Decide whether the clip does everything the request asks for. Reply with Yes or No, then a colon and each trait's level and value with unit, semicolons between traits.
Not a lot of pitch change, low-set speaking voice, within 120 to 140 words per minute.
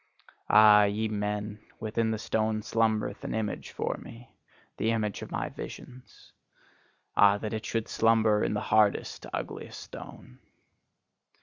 Yes: narrow, 1.2 semitones; low, 110 Hz; slow, 135 wpm